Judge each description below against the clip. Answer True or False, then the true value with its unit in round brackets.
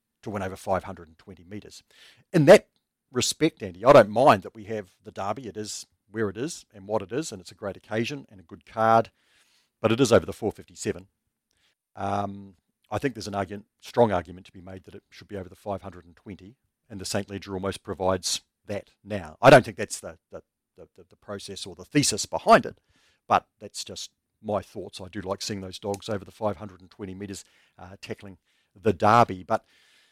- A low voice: True (100 Hz)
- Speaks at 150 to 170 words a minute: False (205 wpm)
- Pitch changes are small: True (2.1 semitones)